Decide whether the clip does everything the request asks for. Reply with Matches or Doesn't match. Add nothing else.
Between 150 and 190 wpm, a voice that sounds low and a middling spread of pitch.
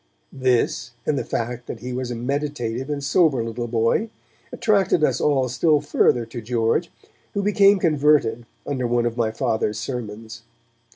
Matches